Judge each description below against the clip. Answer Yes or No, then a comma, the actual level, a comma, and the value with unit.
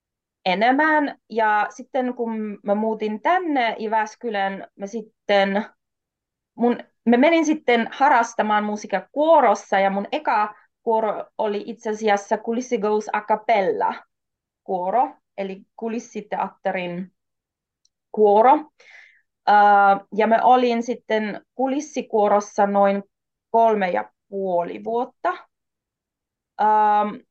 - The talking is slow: Yes, slow, 90 wpm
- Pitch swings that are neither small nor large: Yes, average, 3.1 semitones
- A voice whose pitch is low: No, high, 220 Hz